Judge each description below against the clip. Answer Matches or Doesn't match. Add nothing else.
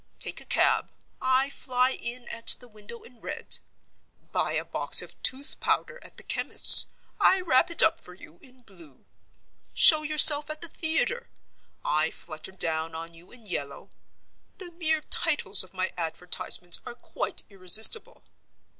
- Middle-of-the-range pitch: Doesn't match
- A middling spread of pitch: Doesn't match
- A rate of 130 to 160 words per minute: Matches